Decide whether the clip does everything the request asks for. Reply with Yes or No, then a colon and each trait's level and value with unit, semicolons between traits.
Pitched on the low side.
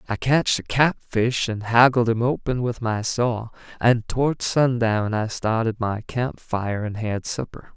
Yes: low, 115 Hz